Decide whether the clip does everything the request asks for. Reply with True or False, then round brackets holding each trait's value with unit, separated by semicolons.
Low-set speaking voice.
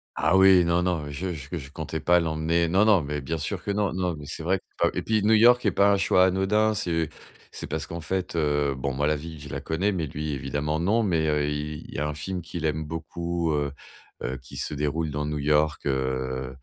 True (80 Hz)